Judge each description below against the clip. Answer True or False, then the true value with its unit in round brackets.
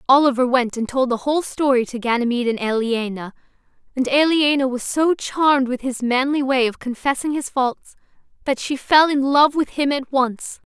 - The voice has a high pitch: True (265 Hz)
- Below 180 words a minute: False (185 wpm)